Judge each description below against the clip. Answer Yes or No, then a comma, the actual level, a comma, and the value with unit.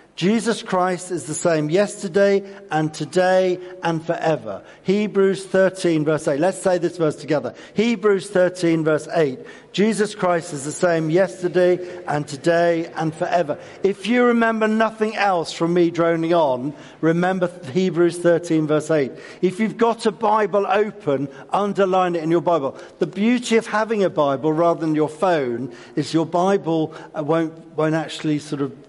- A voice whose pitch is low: No, medium, 175 Hz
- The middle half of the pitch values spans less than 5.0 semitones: Yes, average, 3.7 semitones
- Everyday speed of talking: Yes, average, 160 wpm